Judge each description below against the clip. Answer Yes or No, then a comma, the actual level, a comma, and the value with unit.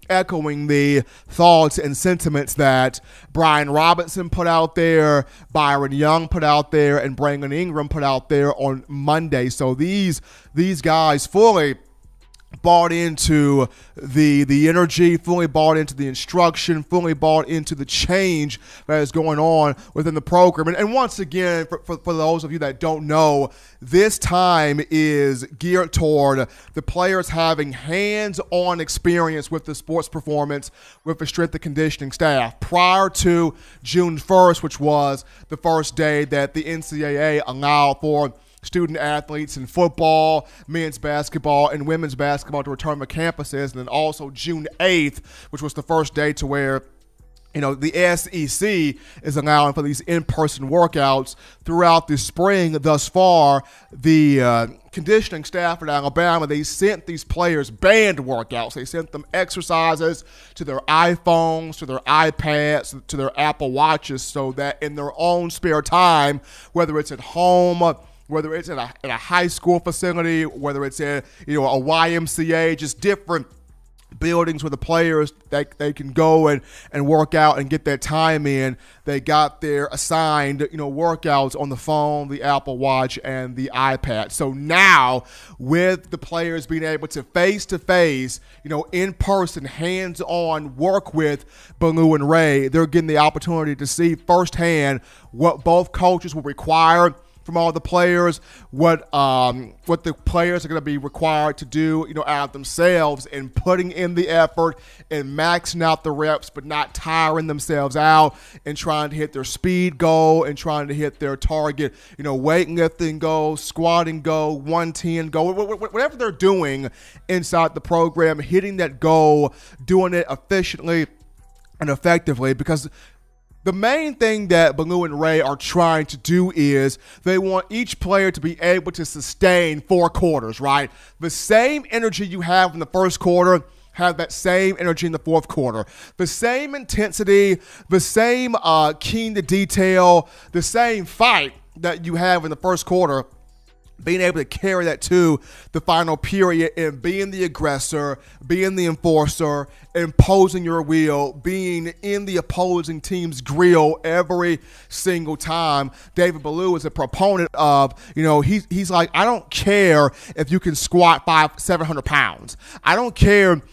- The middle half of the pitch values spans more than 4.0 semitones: No, average, 3.1 semitones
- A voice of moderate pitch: Yes, medium, 160 Hz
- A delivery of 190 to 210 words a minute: No, average, 160 wpm